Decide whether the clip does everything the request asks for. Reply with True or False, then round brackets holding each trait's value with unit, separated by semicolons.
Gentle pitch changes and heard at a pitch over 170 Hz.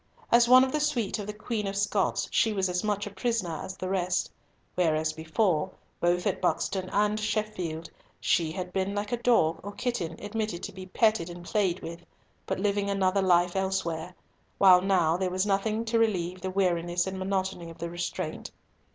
False (3.1 semitones; 190 Hz)